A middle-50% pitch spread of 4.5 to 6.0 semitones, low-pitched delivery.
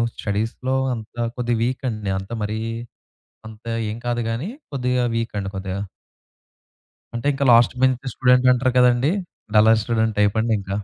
No: average, 2.7 semitones; low, 115 Hz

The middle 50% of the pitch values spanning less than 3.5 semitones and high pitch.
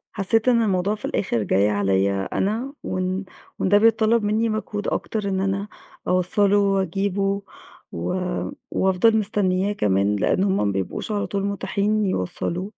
Yes: narrow, 2.4 semitones; high, 195 Hz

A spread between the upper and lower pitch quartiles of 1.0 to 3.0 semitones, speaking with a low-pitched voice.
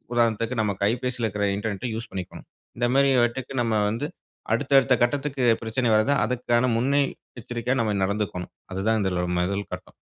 No: average, 3.4 semitones; low, 115 Hz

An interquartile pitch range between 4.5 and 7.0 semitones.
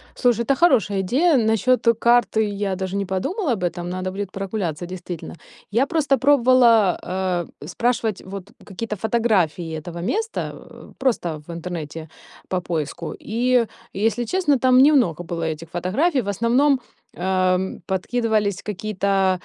Yes: average, 5.2 semitones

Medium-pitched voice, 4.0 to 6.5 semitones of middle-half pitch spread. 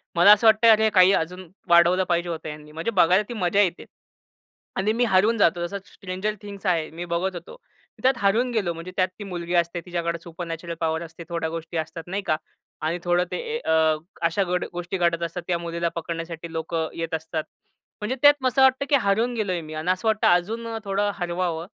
No: medium, 175 Hz; average, 3.3 semitones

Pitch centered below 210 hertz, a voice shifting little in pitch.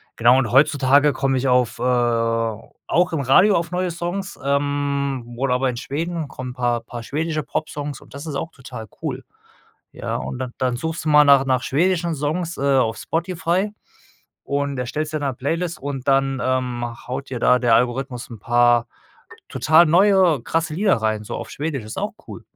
No: medium, 140 Hz; average, 4.1 semitones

